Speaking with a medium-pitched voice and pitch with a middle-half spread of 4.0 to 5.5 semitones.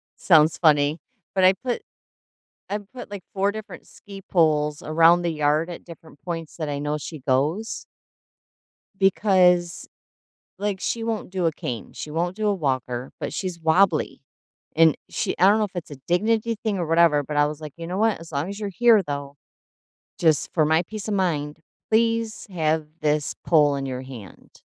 Yes: medium, 170 Hz; average, 4.8 semitones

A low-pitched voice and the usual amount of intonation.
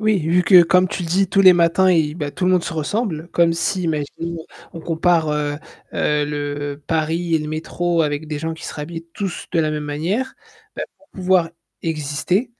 No: medium, 165 Hz; average, 3.0 semitones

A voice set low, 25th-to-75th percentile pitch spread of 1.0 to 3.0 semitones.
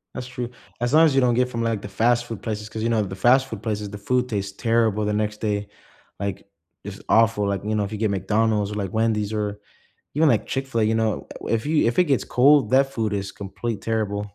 Yes: low, 110 Hz; average, 2.7 semitones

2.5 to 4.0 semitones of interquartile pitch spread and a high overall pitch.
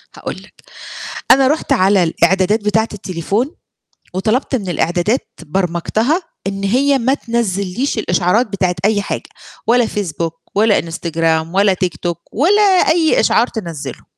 No: average, 5.2 semitones; high, 200 Hz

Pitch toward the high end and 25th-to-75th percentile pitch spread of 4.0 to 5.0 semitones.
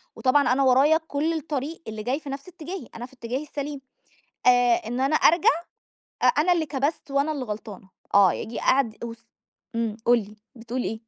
Yes: very high, 265 Hz; average, 4.4 semitones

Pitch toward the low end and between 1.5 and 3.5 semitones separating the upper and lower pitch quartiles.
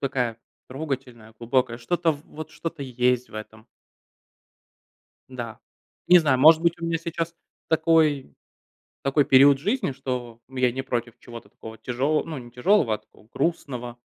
No: low, 130 Hz; average, 4.7 semitones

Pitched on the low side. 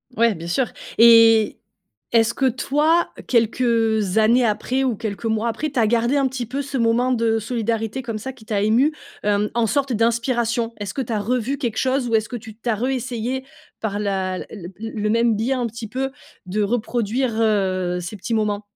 No: high, 230 Hz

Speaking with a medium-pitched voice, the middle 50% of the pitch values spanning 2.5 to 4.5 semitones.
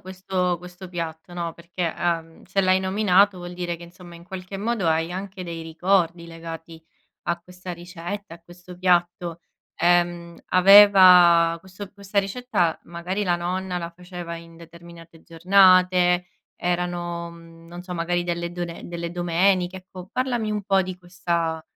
No: medium, 175 Hz; narrow, 1.6 semitones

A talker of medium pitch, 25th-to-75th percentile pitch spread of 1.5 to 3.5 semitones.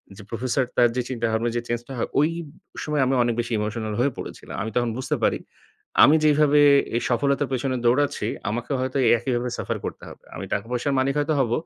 No: low, 125 Hz; average, 2.9 semitones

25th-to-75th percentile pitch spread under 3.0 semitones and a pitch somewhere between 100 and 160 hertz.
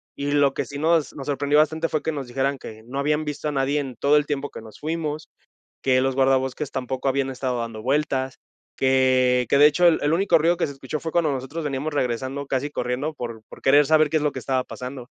Yes: narrow, 2.4 semitones; medium, 140 Hz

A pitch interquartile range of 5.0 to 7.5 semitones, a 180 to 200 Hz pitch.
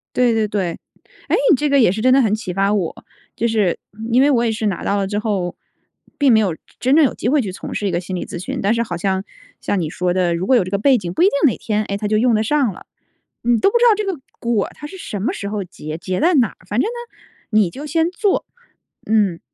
No: wide, 5.4 semitones; high, 215 Hz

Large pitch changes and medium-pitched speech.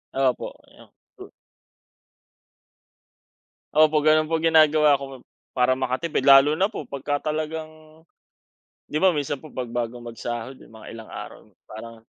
No: average, 3.6 semitones; medium, 150 Hz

